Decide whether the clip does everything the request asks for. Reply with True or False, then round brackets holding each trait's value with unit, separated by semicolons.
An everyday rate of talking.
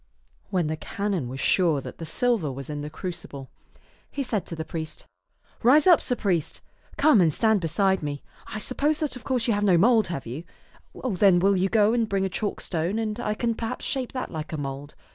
False (220 wpm)